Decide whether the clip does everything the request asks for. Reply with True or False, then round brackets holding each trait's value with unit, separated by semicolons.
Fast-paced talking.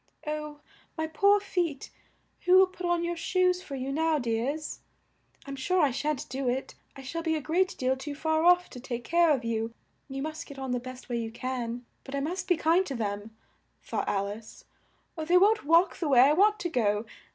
True (220 wpm)